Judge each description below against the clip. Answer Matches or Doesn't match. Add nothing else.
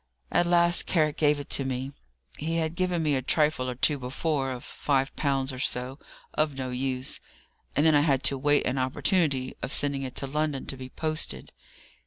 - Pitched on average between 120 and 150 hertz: Matches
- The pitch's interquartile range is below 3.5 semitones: Matches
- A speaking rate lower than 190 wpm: Doesn't match